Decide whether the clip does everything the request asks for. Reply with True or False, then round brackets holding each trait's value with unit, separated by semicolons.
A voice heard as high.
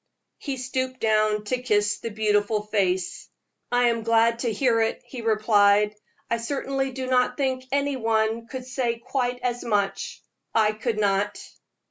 True (230 Hz)